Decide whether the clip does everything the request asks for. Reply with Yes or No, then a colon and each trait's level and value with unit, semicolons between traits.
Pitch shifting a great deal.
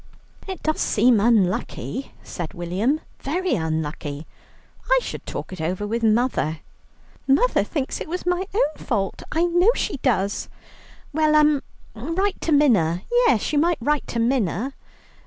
Yes: wide, 8.2 semitones